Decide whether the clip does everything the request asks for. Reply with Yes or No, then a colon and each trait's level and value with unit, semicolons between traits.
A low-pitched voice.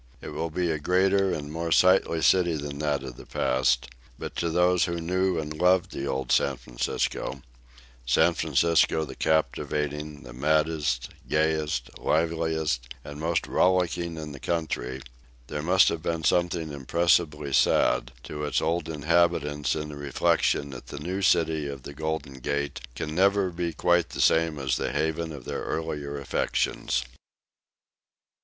Yes: very low, 80 Hz